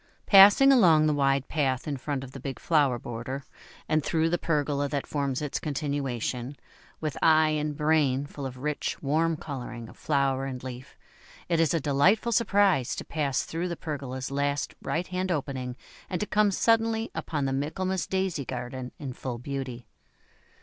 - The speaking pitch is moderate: Yes, medium, 145 Hz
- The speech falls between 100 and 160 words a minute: No, average, 170 wpm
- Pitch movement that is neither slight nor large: Yes, average, 3.6 semitones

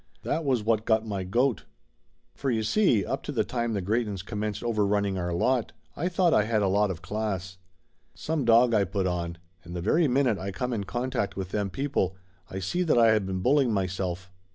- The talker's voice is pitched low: Yes, low, 105 Hz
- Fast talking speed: Yes, fast, 220 wpm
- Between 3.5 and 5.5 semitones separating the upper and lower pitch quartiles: Yes, average, 4.3 semitones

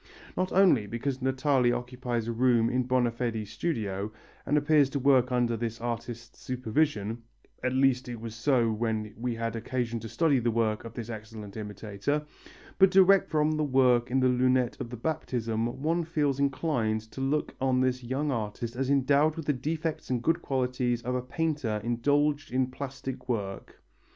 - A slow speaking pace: No, average, 175 wpm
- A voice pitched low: Yes, low, 125 Hz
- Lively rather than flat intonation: No, average, 3.5 semitones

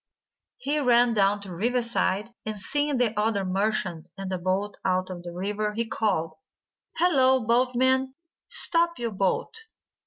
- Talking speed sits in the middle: Yes, average, 150 wpm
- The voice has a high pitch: Yes, high, 215 Hz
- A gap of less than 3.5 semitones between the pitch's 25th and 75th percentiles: No, average, 4.7 semitones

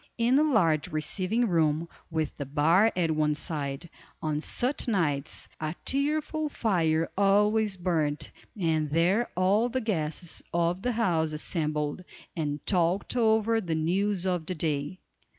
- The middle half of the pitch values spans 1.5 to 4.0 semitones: No, average, 5.3 semitones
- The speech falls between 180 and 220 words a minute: No, average, 140 wpm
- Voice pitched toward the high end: No, medium, 175 Hz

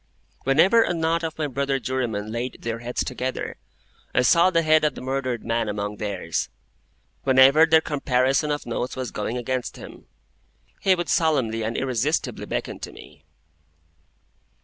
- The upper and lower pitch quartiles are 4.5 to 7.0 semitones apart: Yes, average, 4.8 semitones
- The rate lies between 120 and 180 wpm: Yes, average, 155 wpm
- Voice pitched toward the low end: Yes, low, 130 Hz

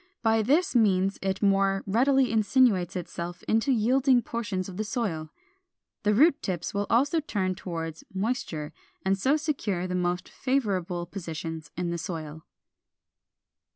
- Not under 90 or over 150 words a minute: Yes, average, 140 wpm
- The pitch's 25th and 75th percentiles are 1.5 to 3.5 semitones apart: No, average, 5.1 semitones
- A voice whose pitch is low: No, high, 195 Hz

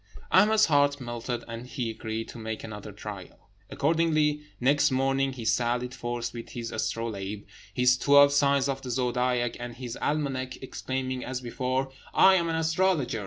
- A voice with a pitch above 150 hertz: No, low, 130 Hz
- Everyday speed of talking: Yes, average, 160 wpm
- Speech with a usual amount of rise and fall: Yes, average, 3.2 semitones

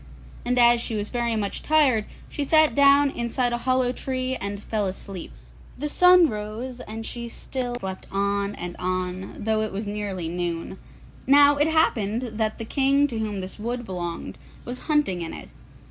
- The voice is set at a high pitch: Yes, high, 225 Hz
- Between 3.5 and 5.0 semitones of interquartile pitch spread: Yes, average, 4.4 semitones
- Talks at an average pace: Yes, average, 175 wpm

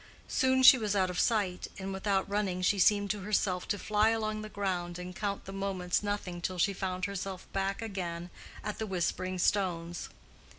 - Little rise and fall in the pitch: Yes, narrow, 2.2 semitones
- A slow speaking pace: No, average, 185 wpm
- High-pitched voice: Yes, high, 195 Hz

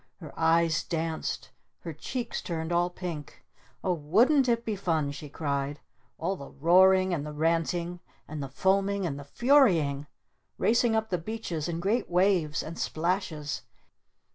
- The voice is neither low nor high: Yes, medium, 170 Hz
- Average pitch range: Yes, average, 3.9 semitones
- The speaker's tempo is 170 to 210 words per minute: No, average, 150 wpm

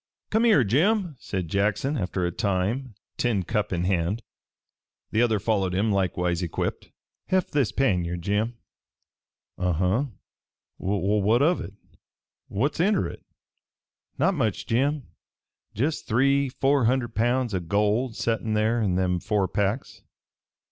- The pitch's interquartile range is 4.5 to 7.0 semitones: Yes, wide, 5.6 semitones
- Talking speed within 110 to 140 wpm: Yes, slow, 135 wpm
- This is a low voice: Yes, low, 110 Hz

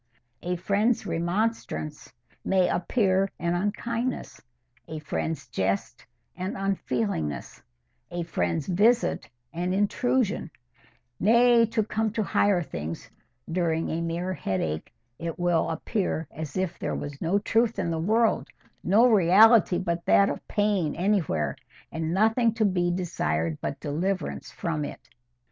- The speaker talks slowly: Yes, slow, 125 wpm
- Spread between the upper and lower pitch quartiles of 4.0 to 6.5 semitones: Yes, average, 5.0 semitones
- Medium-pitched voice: Yes, medium, 175 Hz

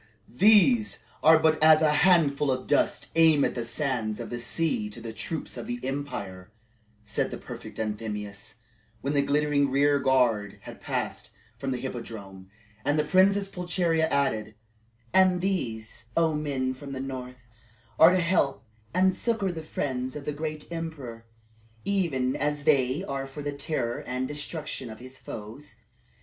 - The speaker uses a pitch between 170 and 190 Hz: No, medium, 140 Hz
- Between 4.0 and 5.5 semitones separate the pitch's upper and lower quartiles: Yes, average, 4.5 semitones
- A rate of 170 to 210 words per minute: No, average, 160 wpm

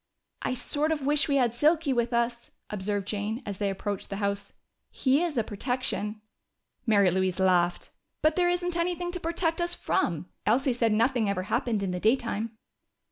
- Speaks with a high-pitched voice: Yes, high, 235 Hz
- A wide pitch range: Yes, wide, 6.5 semitones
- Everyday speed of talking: Yes, average, 180 wpm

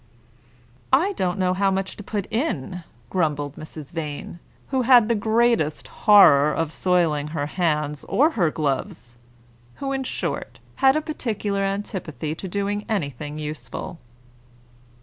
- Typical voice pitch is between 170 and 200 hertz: Yes, medium, 185 Hz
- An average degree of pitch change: No, wide, 6.1 semitones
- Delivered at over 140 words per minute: No, slow, 135 wpm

